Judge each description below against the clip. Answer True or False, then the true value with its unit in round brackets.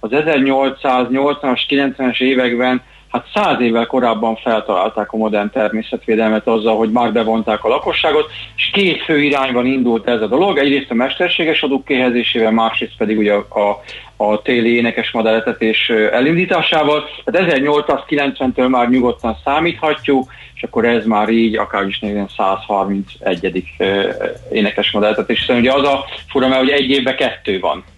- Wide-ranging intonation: False (3.7 semitones)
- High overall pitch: False (120 Hz)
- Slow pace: False (140 wpm)